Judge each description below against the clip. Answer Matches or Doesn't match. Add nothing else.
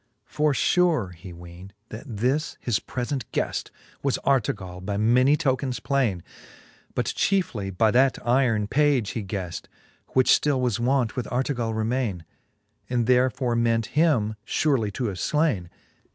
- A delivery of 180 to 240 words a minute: Doesn't match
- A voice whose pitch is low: Matches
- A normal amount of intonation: Matches